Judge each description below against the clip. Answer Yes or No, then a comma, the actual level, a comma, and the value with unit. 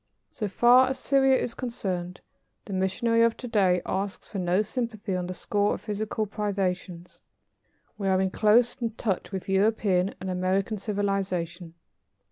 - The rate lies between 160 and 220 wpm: No, average, 150 wpm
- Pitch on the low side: No, high, 200 Hz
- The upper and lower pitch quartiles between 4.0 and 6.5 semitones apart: No, average, 3.2 semitones